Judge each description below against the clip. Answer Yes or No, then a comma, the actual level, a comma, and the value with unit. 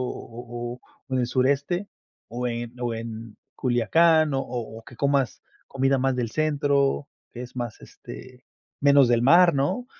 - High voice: No, low, 125 Hz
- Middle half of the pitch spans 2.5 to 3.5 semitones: Yes, average, 2.9 semitones